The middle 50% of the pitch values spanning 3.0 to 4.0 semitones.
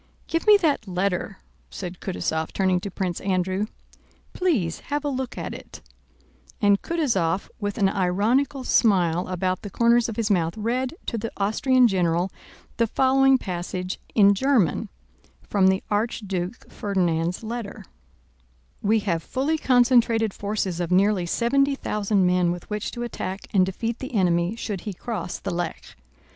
No: average, 4.6 semitones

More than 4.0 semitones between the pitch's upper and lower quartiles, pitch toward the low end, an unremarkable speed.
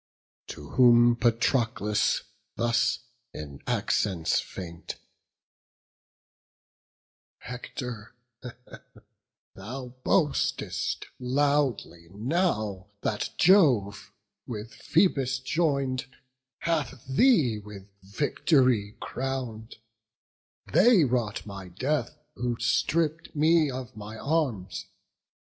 No: average, 5.2 semitones; low, 125 Hz; slow, 75 wpm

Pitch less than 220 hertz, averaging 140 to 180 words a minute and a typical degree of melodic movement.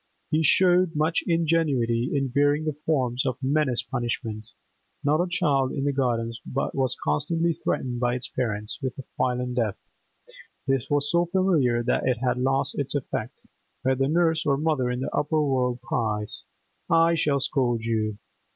Yes: low, 135 Hz; average, 170 wpm; average, 4.0 semitones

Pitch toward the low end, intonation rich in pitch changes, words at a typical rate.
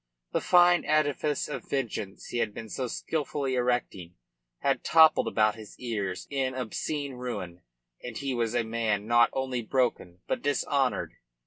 No: low, 125 Hz; average, 4.1 semitones; average, 150 wpm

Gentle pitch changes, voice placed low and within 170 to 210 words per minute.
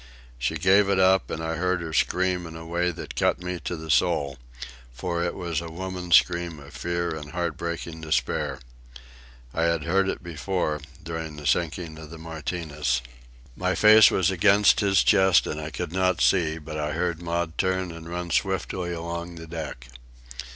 Yes: narrow, 2.2 semitones; very low, 85 Hz; average, 185 wpm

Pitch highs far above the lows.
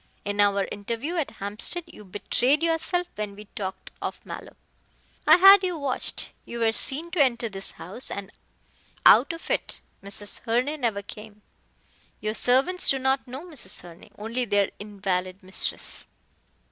Yes: wide, 6.1 semitones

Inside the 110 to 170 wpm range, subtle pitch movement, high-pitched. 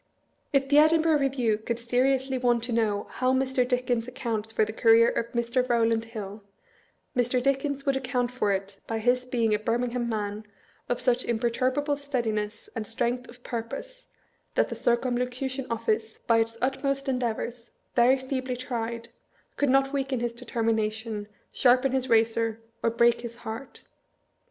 Yes: average, 155 wpm; narrow, 2.3 semitones; high, 245 Hz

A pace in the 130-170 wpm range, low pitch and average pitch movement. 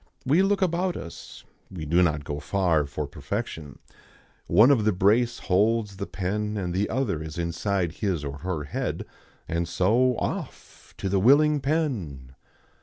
No: average, 160 wpm; very low, 95 Hz; wide, 6.3 semitones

